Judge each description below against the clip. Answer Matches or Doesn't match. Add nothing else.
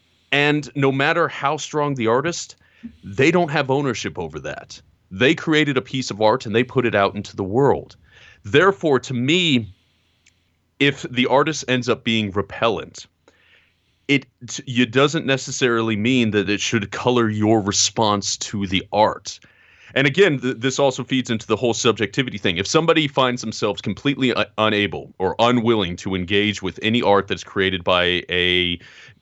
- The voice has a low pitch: Matches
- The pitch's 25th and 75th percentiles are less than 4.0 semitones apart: Doesn't match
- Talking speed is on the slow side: Doesn't match